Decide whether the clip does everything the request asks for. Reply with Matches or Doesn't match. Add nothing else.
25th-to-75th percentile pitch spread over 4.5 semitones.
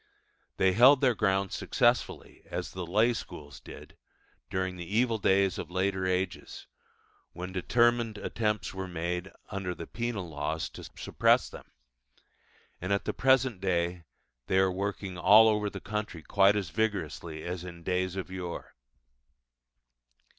Doesn't match